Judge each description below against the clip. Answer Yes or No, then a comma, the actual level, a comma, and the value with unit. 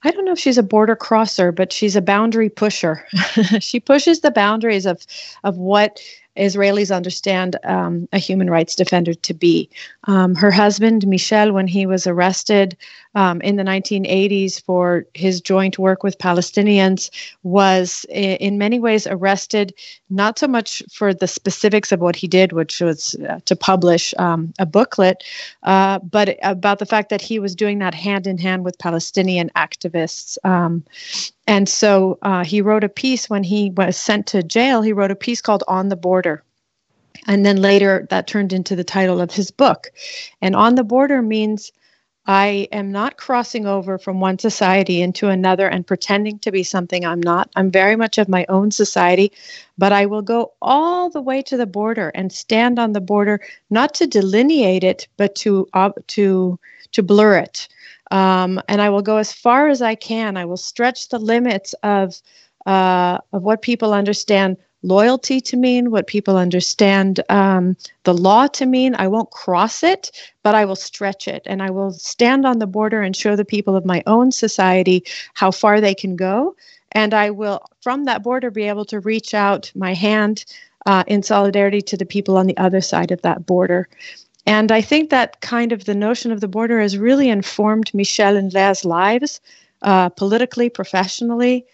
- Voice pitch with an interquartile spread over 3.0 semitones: No, narrow, 2.6 semitones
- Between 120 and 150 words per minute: No, average, 185 wpm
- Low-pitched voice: No, high, 200 Hz